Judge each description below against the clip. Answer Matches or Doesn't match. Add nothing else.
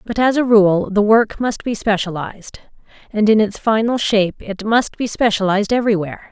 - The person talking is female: Matches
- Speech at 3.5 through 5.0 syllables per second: Doesn't match